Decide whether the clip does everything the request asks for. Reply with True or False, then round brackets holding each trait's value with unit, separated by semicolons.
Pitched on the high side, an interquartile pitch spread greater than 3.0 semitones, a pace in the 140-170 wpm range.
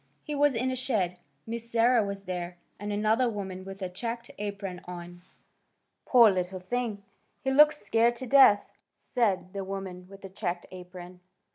True (200 Hz; 4.2 semitones; 165 wpm)